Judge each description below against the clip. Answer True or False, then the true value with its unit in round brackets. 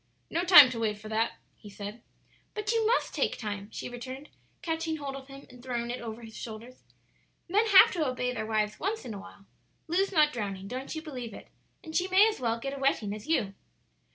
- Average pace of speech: False (215 wpm)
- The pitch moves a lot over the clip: True (6.5 semitones)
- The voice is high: True (255 Hz)